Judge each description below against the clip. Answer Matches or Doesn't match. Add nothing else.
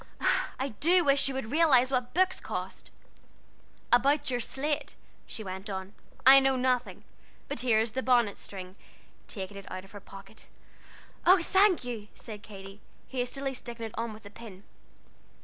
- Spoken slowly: Doesn't match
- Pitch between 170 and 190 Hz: Doesn't match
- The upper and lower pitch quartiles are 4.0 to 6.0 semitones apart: Matches